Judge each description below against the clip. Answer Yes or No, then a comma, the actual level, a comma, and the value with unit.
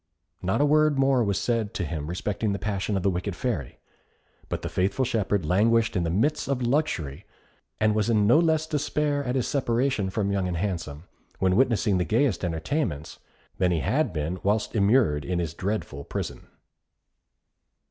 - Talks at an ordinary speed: Yes, average, 180 wpm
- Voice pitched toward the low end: Yes, low, 105 Hz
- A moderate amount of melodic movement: No, wide, 5.9 semitones